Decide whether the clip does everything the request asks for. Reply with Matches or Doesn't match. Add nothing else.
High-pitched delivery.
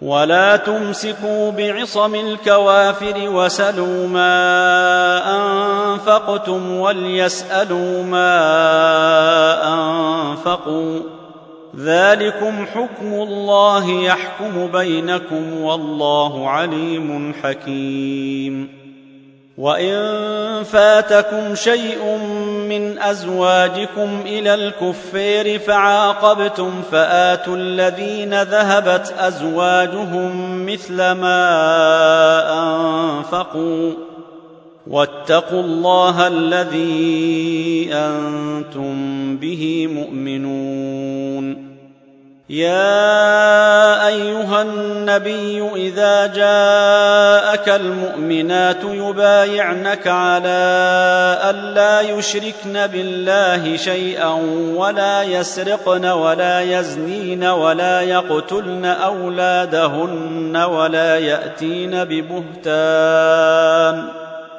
Doesn't match